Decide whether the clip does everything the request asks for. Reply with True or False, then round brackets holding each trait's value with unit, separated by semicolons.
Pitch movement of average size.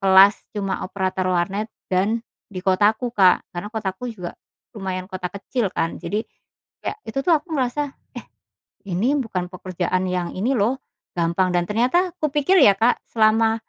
True (4.1 semitones)